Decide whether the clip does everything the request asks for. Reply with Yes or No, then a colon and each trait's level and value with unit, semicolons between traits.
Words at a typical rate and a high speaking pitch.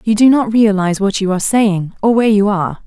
No: fast, 250 wpm; high, 205 Hz